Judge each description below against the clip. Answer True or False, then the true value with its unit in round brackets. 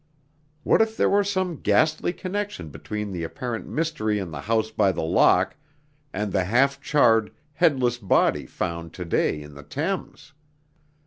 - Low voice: True (110 Hz)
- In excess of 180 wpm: False (155 wpm)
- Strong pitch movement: True (9.0 semitones)